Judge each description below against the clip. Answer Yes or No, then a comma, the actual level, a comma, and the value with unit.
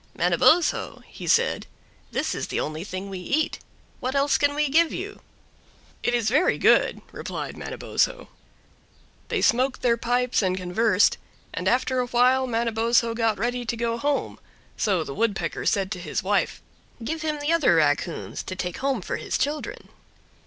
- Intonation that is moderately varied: No, wide, 5.7 semitones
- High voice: Yes, high, 235 Hz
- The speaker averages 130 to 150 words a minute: No, average, 165 wpm